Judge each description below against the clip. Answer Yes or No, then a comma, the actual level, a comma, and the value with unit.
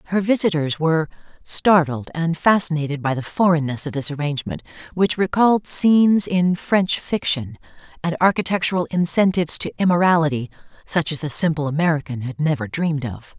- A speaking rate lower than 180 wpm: Yes, average, 145 wpm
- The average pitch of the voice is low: No, medium, 165 Hz